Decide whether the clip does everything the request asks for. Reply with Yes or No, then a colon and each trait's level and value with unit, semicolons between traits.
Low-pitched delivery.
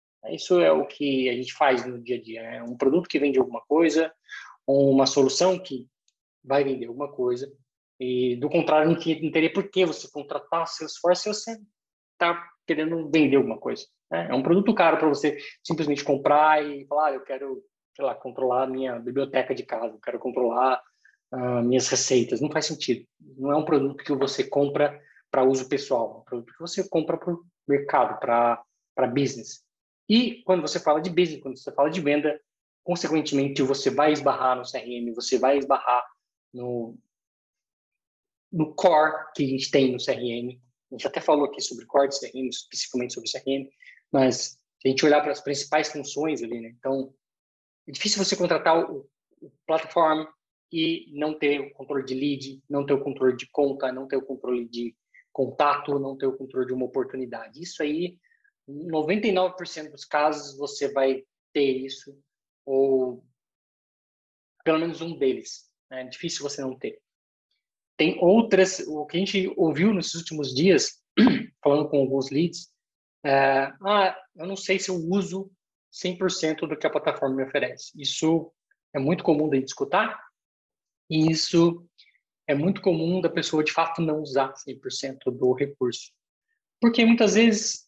No: medium, 145 Hz